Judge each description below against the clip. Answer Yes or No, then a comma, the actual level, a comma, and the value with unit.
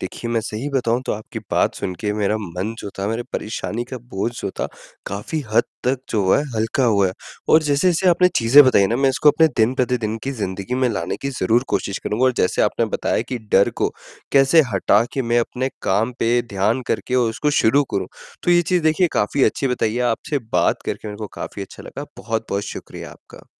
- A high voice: No, low, 120 Hz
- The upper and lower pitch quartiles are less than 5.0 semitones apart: Yes, average, 4.1 semitones